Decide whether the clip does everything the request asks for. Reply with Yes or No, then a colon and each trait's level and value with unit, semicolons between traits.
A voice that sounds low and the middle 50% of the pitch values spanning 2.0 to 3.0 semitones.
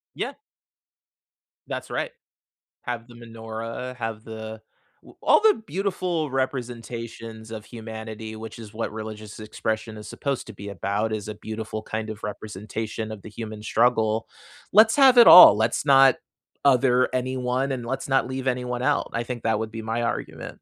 Yes: low, 115 Hz; narrow, 2.6 semitones